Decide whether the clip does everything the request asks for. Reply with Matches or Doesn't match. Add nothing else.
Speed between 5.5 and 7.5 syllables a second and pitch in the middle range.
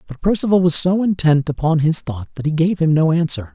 Matches